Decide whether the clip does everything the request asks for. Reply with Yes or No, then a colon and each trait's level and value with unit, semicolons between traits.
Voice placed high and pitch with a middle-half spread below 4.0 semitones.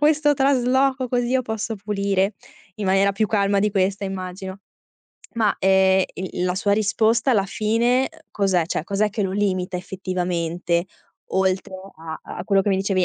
Yes: high, 200 Hz; average, 2.8 semitones